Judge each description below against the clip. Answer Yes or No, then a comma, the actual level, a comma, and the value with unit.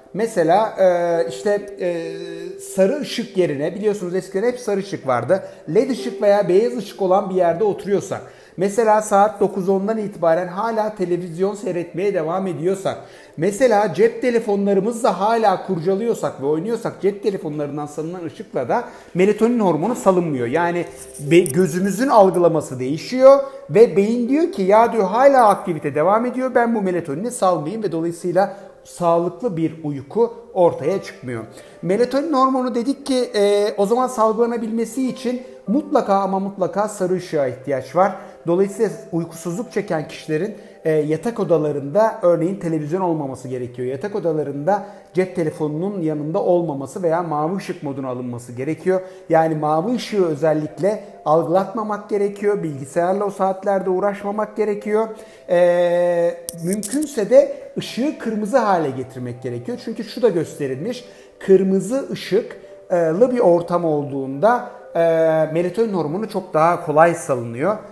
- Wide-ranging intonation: No, average, 4.6 semitones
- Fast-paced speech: No, average, 125 wpm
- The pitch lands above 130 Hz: Yes, high, 190 Hz